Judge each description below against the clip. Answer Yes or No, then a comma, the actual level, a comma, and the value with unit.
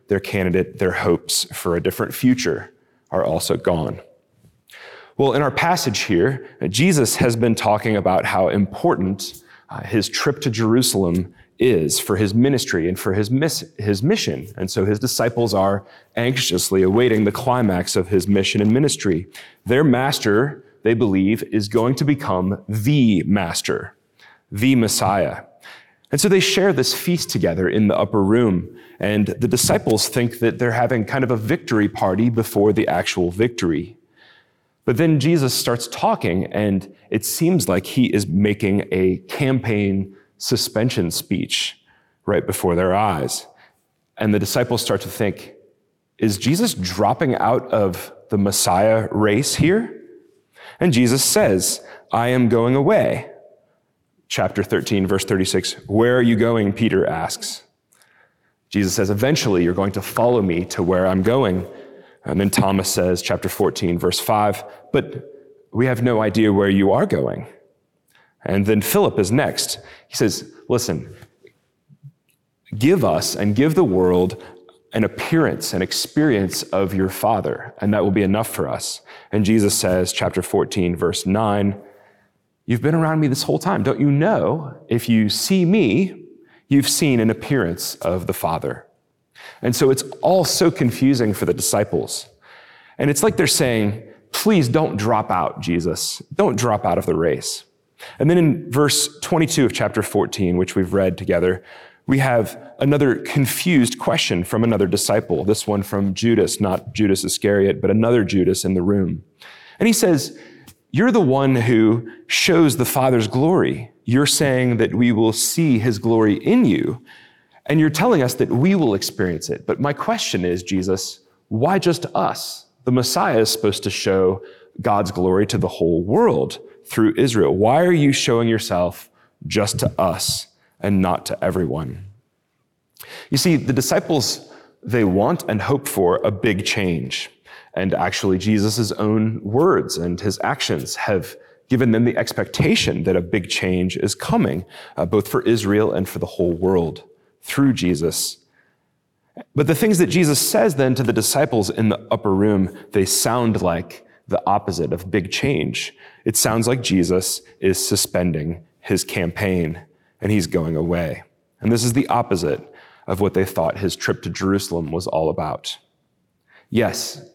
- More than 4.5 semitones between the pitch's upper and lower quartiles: Yes, average, 5.1 semitones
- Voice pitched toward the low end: Yes, low, 110 Hz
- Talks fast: No, average, 160 wpm